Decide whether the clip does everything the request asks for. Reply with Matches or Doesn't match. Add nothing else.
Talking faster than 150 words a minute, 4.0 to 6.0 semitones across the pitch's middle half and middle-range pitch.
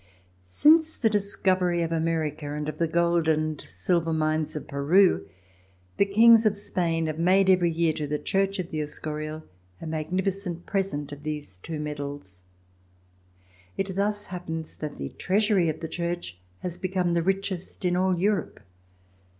Doesn't match